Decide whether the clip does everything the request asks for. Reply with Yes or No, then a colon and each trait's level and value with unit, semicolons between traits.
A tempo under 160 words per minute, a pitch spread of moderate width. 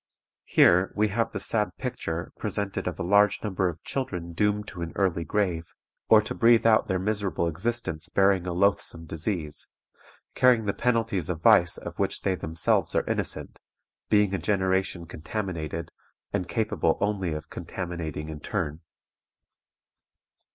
Yes: average, 150 wpm; average, 3.8 semitones